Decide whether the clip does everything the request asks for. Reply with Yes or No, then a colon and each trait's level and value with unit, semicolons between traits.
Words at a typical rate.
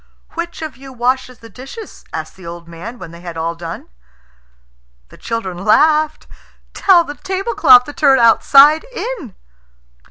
Yes: average, 150 wpm